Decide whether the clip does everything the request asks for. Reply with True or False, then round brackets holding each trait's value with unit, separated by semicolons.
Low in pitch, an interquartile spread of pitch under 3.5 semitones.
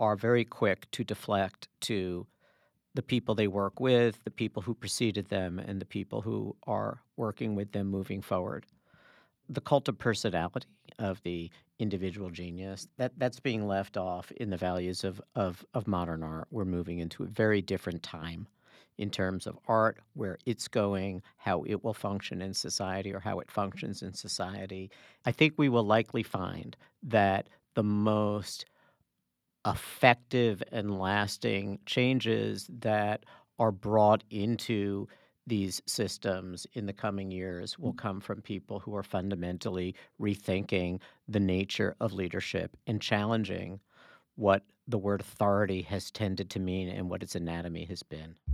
True (100 Hz; 3.0 semitones)